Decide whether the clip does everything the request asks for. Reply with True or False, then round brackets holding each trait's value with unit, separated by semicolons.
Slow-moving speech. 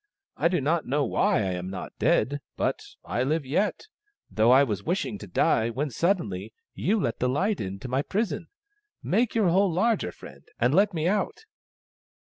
False (190 wpm)